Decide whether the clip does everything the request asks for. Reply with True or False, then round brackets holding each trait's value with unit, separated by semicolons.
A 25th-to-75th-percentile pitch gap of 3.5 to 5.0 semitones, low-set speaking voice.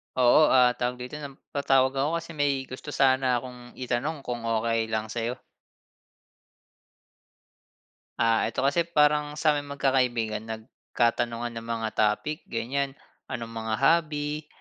True (3.8 semitones; 130 Hz)